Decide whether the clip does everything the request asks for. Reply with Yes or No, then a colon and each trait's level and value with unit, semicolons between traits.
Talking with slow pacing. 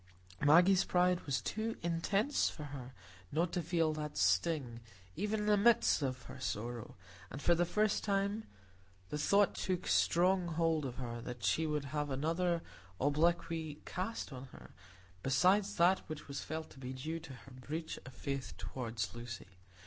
No: average, 165 wpm